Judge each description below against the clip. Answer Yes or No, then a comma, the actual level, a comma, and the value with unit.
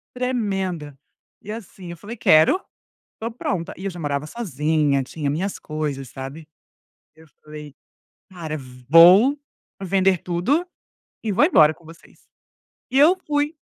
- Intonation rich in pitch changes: Yes, wide, 6.0 semitones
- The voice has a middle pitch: Yes, medium, 175 Hz